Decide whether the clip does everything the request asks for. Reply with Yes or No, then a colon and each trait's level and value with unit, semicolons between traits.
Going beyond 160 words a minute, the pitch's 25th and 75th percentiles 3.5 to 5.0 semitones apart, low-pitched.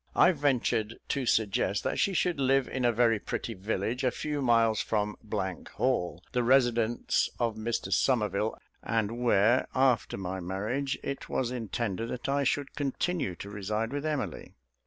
No: average, 155 wpm; average, 3.9 semitones; low, 120 Hz